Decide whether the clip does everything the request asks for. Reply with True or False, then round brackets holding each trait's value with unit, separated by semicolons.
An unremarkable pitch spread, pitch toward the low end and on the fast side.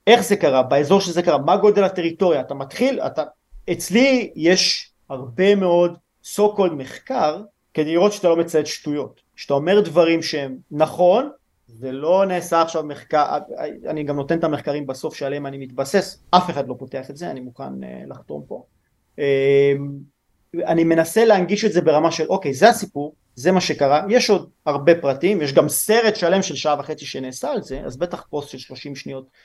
False (4.8 semitones; 160 Hz; 180 wpm)